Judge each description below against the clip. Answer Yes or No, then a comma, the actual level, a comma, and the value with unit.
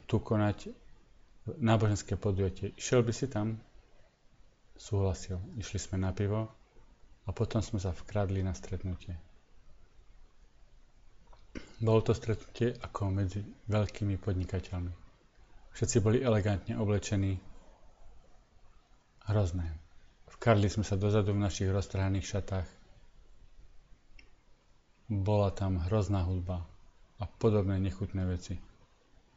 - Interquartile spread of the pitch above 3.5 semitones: No, average, 2.7 semitones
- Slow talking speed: Yes, slow, 100 wpm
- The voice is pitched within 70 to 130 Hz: Yes, low, 100 Hz